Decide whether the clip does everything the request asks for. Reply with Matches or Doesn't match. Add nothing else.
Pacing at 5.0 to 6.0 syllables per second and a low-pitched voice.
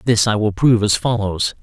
Matches